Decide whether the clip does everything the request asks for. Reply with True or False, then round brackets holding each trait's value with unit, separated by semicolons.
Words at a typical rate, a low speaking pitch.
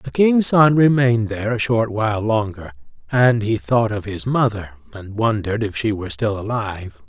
True (185 wpm; 115 Hz)